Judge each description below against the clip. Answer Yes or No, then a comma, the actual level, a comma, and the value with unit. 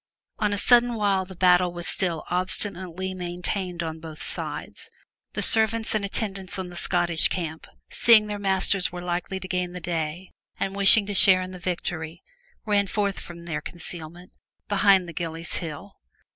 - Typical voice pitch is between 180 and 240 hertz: Yes, medium, 185 Hz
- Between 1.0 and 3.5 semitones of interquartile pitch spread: Yes, narrow, 2.4 semitones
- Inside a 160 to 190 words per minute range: Yes, average, 170 wpm